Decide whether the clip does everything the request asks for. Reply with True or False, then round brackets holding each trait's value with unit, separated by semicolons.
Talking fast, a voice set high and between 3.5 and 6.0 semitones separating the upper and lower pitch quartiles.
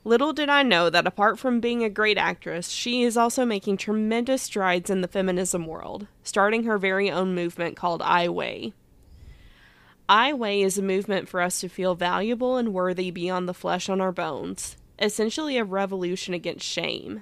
False (180 wpm; 195 Hz; 3.8 semitones)